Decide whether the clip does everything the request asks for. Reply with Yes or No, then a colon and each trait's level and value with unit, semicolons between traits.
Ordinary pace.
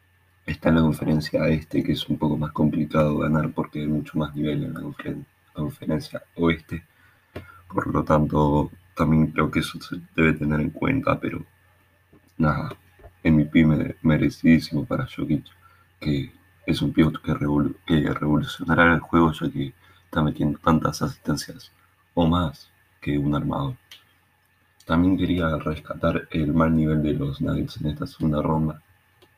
Yes: average, 155 wpm